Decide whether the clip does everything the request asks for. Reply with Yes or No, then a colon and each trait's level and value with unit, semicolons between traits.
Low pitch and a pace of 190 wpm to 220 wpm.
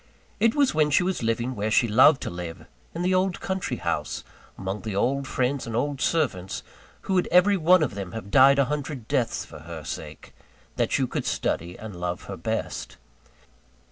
Yes: low, 130 Hz; average, 195 wpm